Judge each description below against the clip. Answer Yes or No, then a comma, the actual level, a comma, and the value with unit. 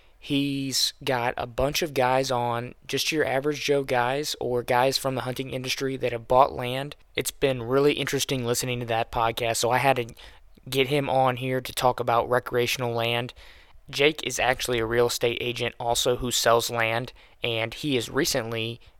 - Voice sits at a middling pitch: No, low, 125 Hz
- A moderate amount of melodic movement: No, narrow, 2.2 semitones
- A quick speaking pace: No, average, 185 wpm